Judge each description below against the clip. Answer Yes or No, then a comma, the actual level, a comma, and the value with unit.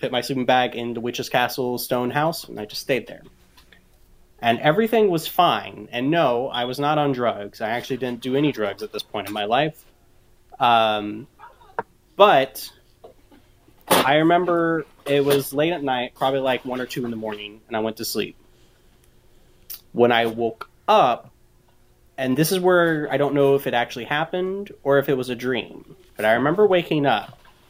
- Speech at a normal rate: Yes, average, 185 wpm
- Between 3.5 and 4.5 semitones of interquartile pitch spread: Yes, average, 4.0 semitones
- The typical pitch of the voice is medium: No, low, 130 Hz